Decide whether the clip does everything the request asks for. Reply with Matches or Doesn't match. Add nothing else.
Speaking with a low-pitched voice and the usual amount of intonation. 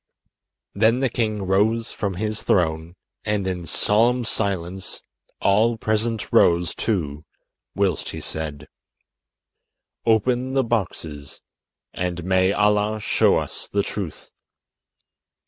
Matches